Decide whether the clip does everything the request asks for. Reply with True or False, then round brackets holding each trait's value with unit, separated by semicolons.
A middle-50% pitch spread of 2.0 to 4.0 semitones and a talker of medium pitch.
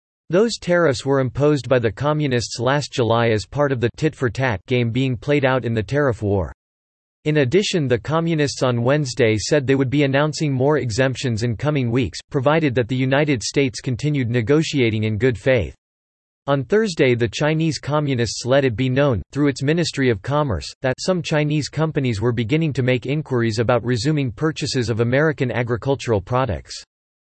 False (3.6 semitones; 130 Hz)